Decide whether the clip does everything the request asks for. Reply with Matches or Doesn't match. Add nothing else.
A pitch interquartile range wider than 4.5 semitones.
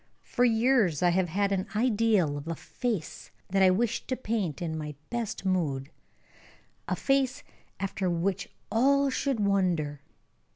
Matches